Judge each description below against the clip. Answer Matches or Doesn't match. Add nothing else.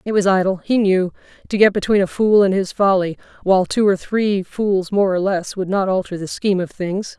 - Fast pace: Matches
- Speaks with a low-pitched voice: Doesn't match